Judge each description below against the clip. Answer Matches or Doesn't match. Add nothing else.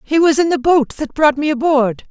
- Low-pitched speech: Doesn't match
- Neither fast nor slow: Doesn't match